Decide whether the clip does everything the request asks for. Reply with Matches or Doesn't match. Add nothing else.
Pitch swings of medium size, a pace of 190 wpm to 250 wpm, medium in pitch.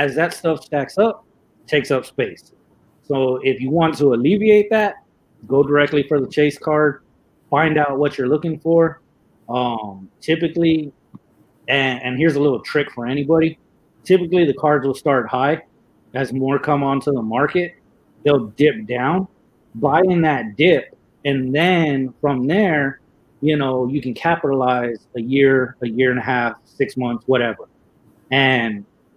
Doesn't match